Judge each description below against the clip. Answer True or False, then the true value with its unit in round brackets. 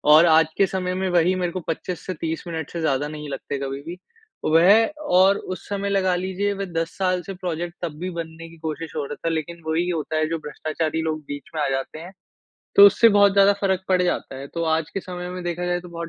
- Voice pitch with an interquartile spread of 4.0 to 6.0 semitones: False (2.7 semitones)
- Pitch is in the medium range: True (170 Hz)